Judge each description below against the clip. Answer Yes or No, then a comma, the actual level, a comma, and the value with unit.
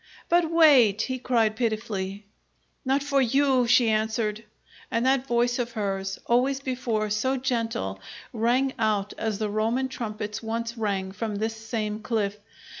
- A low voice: No, high, 230 Hz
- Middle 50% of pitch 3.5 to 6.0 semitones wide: No, average, 3.1 semitones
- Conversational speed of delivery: Yes, average, 145 wpm